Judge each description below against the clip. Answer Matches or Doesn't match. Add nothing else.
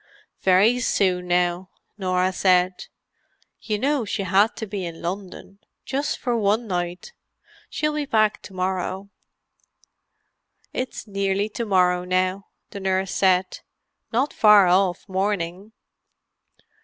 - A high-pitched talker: Matches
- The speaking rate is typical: Doesn't match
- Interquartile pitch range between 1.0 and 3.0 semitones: Matches